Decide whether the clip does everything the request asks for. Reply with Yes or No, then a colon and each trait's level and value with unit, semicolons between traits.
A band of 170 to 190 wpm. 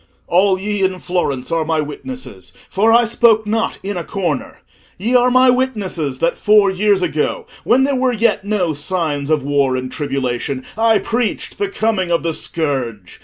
Yes: average, 175 wpm